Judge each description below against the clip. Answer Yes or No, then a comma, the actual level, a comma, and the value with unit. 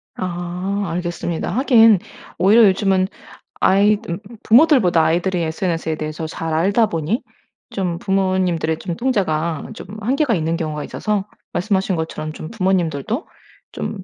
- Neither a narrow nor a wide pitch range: Yes, average, 4.1 semitones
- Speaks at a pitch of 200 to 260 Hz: No, medium, 185 Hz